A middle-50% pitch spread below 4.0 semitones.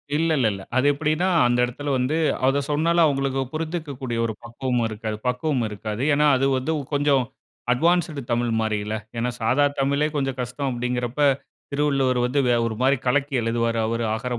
Yes: average, 3.4 semitones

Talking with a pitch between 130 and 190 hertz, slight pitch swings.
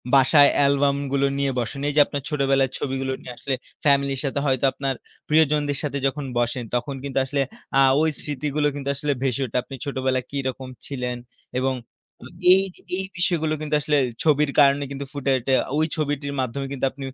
Yes: medium, 140 Hz; narrow, 1.6 semitones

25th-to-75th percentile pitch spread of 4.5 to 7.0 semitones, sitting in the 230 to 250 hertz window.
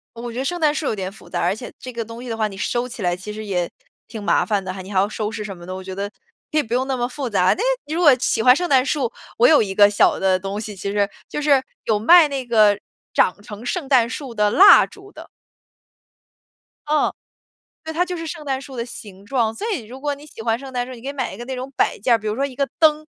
Yes: average, 5.1 semitones; high, 240 Hz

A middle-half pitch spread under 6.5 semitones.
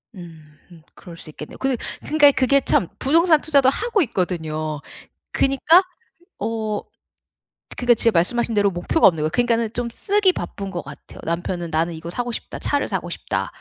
No: wide, 8.1 semitones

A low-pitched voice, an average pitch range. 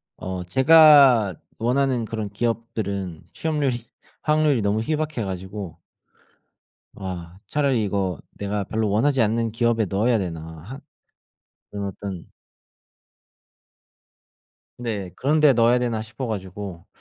Yes: low, 110 Hz; average, 4.5 semitones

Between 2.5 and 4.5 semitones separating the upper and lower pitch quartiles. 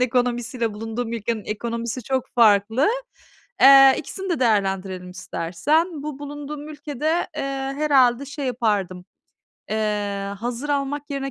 No: average, 5.0 semitones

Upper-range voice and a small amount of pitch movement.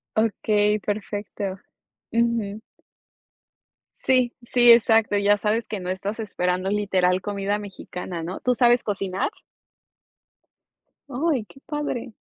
No: high, 210 Hz; average, 3.1 semitones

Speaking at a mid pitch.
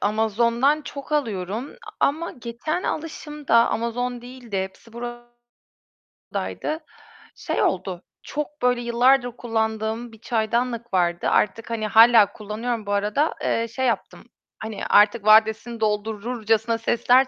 No: high, 235 Hz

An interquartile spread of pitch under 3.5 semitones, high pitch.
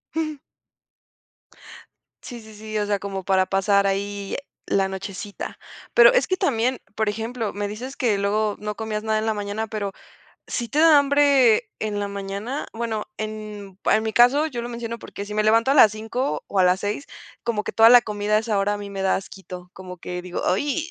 Yes: average, 2.8 semitones; high, 215 Hz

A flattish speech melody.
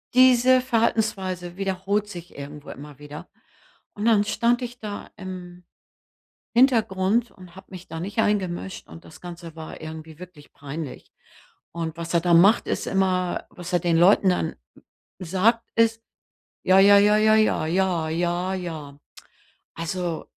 No: average, 3.9 semitones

